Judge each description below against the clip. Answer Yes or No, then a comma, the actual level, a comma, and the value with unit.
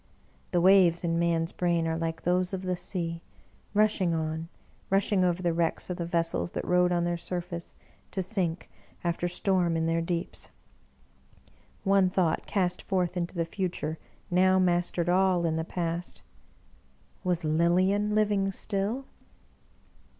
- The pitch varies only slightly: Yes, narrow, 2.0 semitones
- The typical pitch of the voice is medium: Yes, medium, 175 Hz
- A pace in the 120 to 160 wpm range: Yes, average, 150 wpm